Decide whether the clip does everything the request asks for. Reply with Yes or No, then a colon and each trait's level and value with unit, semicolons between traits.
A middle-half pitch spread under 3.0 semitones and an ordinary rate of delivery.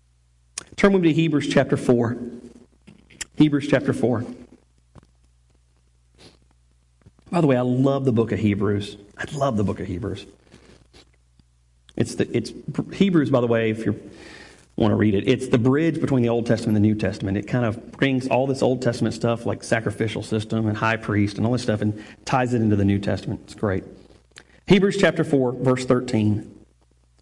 No: average, 4.3 semitones; average, 180 wpm